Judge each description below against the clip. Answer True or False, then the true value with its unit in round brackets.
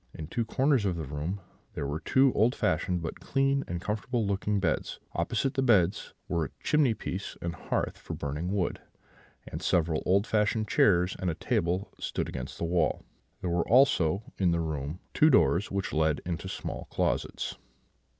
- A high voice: False (95 Hz)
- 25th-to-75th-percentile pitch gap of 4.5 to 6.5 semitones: True (4.8 semitones)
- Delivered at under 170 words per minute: False (175 wpm)